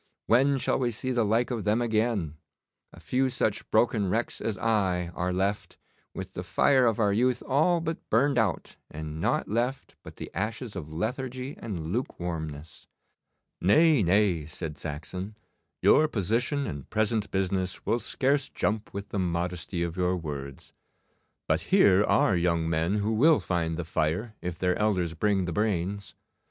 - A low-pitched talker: Yes, low, 100 Hz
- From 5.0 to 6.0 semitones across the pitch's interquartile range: Yes, average, 5.3 semitones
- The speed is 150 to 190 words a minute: Yes, average, 160 wpm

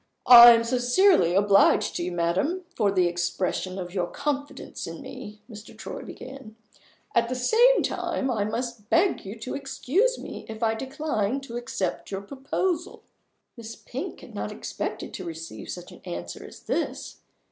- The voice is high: Yes, high, 230 Hz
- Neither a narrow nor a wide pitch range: No, wide, 5.9 semitones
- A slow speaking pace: No, average, 165 wpm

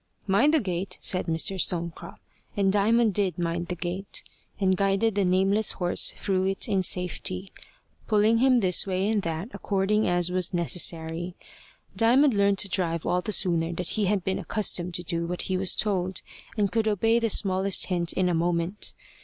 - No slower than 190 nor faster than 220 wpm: No, average, 180 wpm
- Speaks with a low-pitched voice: No, high, 190 Hz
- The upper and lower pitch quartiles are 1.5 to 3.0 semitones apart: Yes, narrow, 2.6 semitones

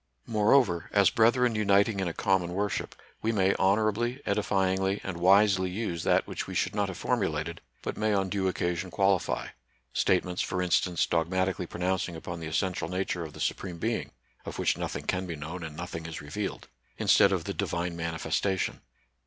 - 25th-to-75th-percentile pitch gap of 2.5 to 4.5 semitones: Yes, average, 2.8 semitones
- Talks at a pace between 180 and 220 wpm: Yes, average, 185 wpm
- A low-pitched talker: Yes, very low, 95 Hz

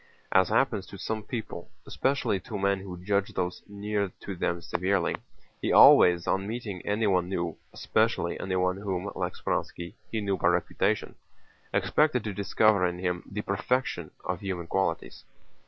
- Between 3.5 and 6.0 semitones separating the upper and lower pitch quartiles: No, narrow, 2.6 semitones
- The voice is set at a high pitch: No, very low, 95 Hz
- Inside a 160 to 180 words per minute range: No, average, 145 wpm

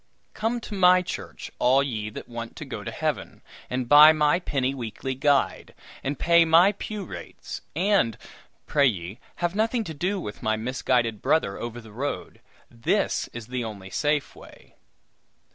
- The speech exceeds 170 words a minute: No, average, 165 wpm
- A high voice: No, medium, 140 Hz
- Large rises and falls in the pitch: Yes, wide, 6.7 semitones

